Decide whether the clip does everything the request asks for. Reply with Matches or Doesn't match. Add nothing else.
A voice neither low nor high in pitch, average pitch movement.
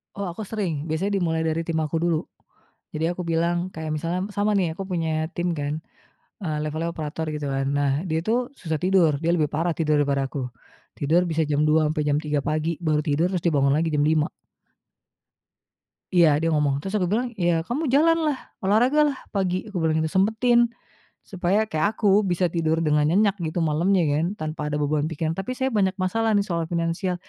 Matches